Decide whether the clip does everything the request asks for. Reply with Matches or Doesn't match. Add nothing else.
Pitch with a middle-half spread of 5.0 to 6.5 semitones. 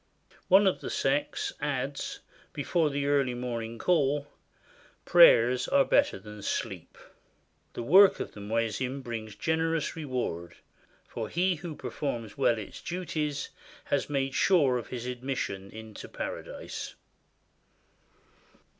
Matches